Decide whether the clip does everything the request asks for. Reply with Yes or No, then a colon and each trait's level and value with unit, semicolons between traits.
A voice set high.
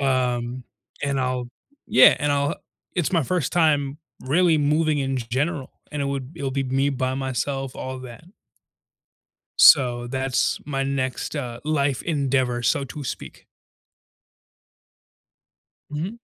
No: low, 135 Hz